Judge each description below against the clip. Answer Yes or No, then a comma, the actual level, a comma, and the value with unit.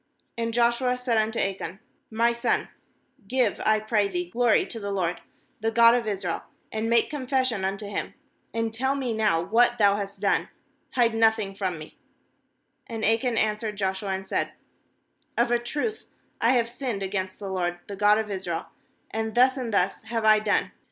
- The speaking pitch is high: Yes, high, 220 Hz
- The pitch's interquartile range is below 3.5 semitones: Yes, average, 3.1 semitones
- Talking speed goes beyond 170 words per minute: Yes, average, 180 wpm